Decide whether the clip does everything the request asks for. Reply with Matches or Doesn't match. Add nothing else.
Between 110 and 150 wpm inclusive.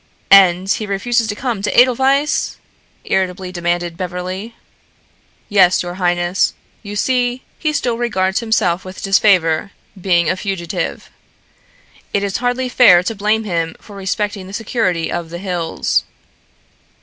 Matches